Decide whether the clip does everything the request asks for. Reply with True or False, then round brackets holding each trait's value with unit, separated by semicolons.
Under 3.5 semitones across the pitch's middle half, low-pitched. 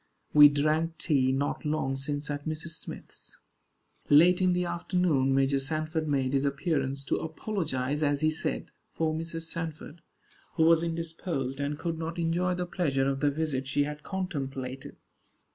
False (3.1 semitones; 155 Hz)